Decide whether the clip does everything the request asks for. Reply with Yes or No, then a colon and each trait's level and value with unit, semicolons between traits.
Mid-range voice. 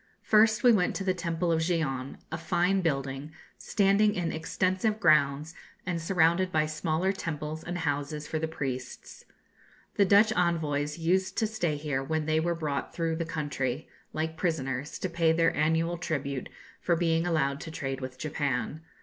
Yes: medium, 160 Hz